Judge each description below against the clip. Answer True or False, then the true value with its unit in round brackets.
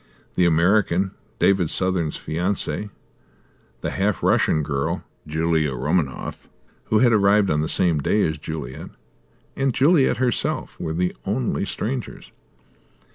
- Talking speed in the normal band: False (125 wpm)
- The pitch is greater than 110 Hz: False (90 Hz)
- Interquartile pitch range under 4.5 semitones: False (5.0 semitones)